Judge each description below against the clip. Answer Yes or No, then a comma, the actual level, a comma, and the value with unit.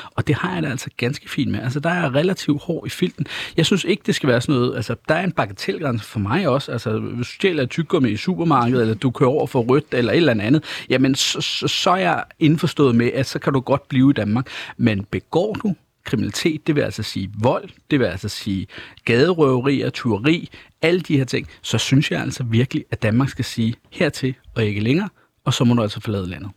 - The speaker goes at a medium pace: No, fast, 240 wpm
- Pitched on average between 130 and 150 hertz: Yes, low, 135 Hz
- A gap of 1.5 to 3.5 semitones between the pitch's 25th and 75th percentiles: No, average, 5.0 semitones